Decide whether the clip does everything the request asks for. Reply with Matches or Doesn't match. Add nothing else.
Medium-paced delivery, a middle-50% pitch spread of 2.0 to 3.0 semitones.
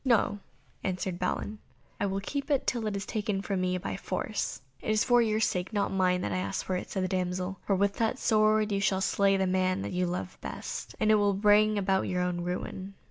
Doesn't match